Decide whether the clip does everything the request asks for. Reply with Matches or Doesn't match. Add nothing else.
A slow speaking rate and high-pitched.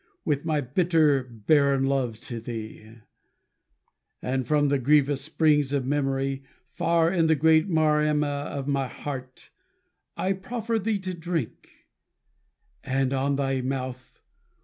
Doesn't match